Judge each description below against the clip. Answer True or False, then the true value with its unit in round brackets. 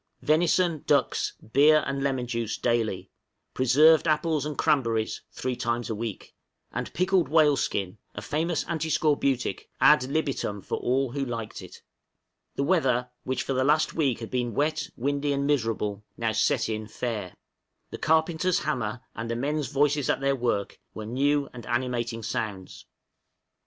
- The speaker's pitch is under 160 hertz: True (135 Hz)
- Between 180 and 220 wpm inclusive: False (155 wpm)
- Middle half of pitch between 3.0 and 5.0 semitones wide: True (4.4 semitones)